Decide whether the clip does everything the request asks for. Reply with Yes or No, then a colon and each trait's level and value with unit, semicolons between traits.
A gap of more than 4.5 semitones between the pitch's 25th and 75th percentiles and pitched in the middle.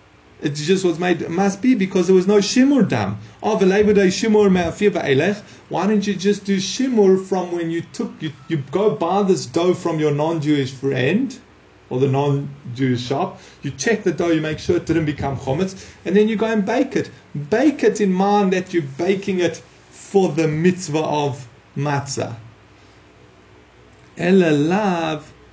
Yes: wide, 5.6 semitones; medium, 175 Hz